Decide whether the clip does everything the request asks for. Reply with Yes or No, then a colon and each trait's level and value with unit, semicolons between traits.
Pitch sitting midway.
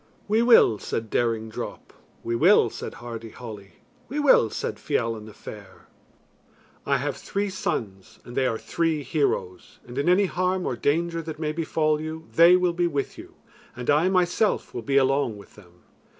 Yes: medium, 145 Hz